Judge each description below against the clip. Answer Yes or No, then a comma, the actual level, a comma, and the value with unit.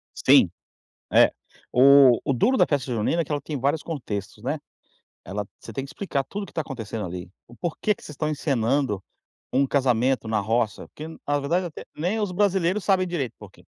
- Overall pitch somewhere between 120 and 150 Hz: Yes, medium, 140 Hz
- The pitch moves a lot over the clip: Yes, wide, 6.2 semitones